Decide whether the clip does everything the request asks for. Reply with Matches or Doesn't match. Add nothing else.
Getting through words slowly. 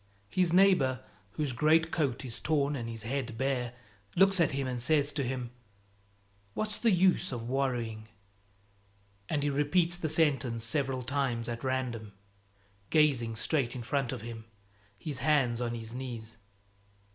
Doesn't match